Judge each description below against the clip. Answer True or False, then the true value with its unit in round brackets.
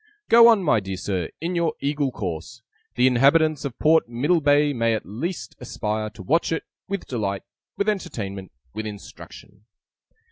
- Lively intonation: True (7.4 semitones)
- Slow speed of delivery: False (155 wpm)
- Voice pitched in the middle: False (130 Hz)